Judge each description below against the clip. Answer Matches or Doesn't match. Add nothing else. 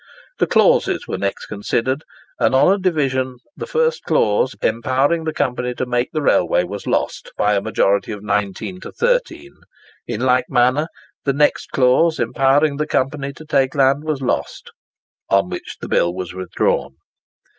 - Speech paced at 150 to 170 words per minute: Matches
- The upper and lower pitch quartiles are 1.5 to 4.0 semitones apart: Doesn't match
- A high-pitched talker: Doesn't match